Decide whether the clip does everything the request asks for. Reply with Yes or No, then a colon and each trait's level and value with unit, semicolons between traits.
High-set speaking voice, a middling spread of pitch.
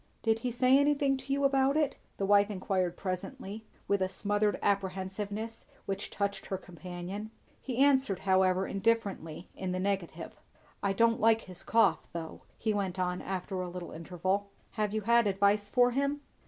Yes: high, 200 Hz; average, 3.5 semitones